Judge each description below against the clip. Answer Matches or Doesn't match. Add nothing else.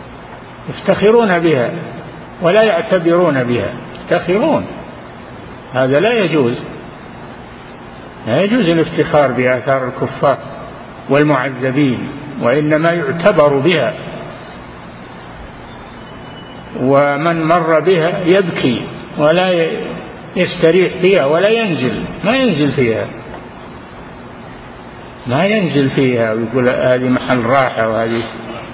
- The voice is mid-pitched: Matches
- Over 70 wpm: Matches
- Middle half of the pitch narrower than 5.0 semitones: Doesn't match